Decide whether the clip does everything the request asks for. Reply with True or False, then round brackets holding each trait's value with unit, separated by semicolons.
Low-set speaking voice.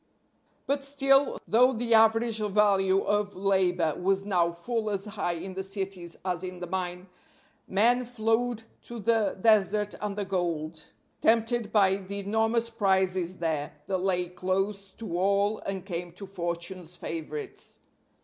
False (195 Hz)